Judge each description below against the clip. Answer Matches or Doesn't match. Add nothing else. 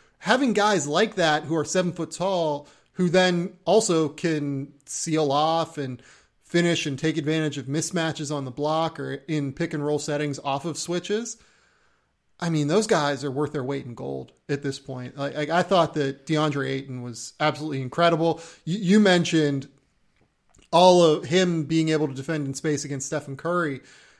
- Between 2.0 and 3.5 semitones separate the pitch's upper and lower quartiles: Matches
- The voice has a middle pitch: Matches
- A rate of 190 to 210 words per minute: Doesn't match